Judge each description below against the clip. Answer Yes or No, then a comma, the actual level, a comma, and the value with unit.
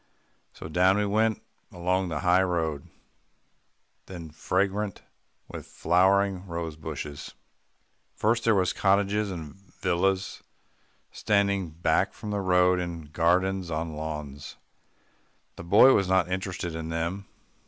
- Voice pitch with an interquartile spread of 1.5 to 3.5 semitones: Yes, average, 3.0 semitones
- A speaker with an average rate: No, slow, 120 wpm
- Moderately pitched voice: No, very low, 90 Hz